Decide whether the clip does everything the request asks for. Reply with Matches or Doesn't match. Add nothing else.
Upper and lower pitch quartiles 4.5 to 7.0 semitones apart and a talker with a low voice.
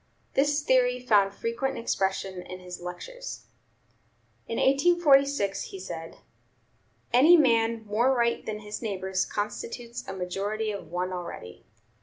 Doesn't match